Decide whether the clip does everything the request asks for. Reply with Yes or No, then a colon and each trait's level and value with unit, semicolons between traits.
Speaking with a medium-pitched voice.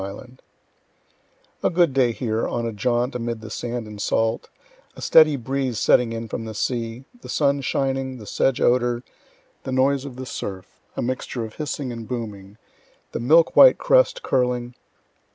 No: low, 125 Hz